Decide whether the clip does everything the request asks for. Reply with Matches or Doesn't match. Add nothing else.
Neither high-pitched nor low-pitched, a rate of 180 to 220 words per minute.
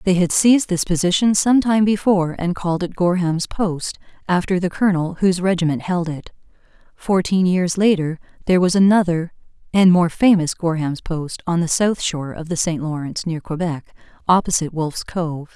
Doesn't match